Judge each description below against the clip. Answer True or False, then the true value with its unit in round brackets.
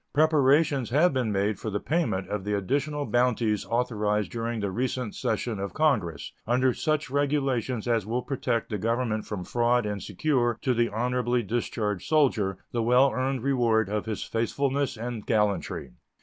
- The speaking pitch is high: False (120 Hz)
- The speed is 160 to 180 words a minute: True (165 wpm)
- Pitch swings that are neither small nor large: True (3.7 semitones)